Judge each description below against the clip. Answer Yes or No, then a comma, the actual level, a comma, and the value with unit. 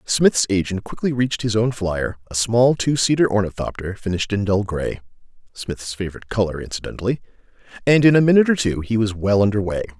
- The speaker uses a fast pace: No, average, 170 wpm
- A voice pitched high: No, low, 105 Hz